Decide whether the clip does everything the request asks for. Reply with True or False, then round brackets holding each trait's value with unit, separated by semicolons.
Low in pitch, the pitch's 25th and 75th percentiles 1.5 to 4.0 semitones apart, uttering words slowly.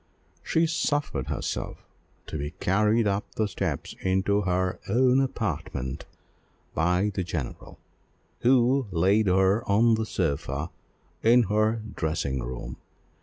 False (100 Hz; 5.4 semitones; 120 wpm)